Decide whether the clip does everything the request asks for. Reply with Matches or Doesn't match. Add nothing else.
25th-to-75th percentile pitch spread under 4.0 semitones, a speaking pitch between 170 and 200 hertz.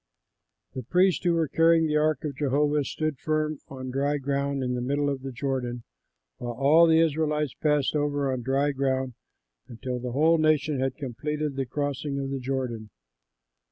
Doesn't match